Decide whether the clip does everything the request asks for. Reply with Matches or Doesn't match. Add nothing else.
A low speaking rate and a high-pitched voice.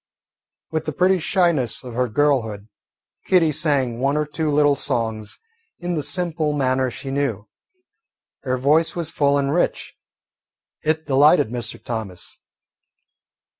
Doesn't match